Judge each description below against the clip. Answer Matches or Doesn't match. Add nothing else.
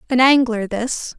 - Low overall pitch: Doesn't match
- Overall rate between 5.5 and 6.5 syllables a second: Doesn't match